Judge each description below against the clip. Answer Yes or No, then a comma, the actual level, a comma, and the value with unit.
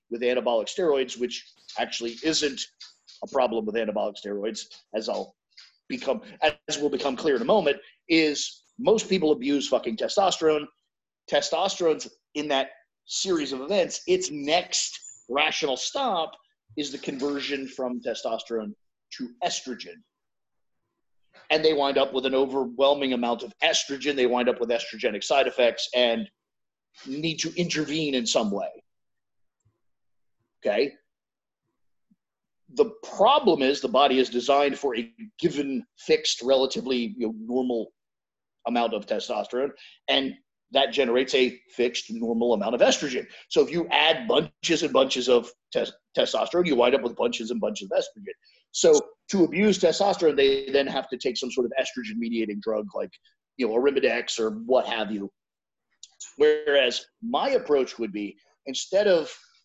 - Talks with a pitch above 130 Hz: Yes, medium, 140 Hz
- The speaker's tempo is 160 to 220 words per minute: No, average, 145 wpm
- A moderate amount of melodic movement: No, wide, 7.0 semitones